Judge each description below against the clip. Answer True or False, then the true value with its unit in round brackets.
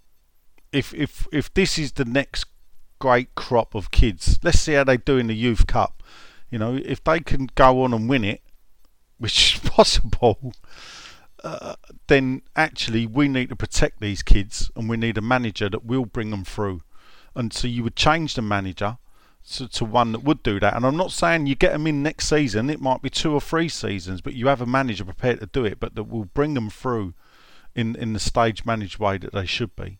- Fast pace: True (215 wpm)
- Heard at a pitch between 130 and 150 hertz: False (120 Hz)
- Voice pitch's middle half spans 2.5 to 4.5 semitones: True (4.2 semitones)